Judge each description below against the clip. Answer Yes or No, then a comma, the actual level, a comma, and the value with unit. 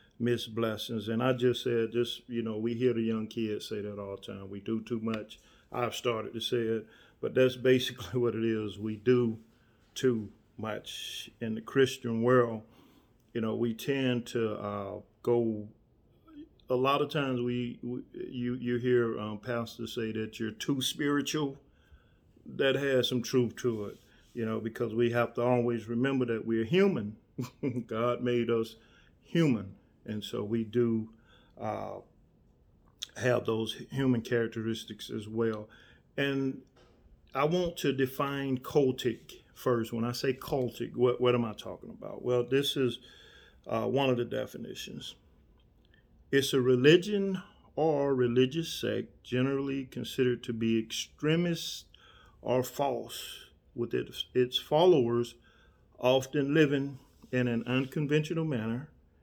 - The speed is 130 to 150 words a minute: Yes, average, 145 wpm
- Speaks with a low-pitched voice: Yes, low, 120 Hz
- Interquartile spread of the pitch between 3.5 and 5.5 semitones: No, narrow, 2.5 semitones